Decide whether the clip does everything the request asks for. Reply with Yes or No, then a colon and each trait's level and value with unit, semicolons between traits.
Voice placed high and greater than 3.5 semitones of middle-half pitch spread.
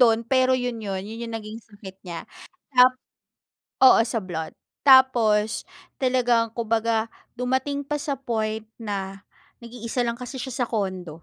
No: high, 230 Hz; average, 3.1 semitones